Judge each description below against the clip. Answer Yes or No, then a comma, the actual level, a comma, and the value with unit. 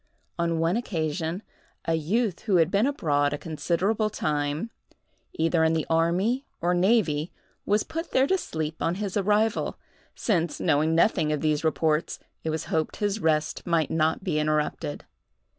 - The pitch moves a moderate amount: Yes, average, 4.6 semitones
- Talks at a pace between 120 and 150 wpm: No, average, 160 wpm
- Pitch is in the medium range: Yes, medium, 165 Hz